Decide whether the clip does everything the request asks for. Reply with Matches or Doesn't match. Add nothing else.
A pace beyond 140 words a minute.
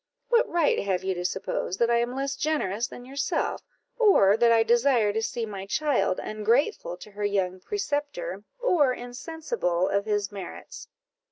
Matches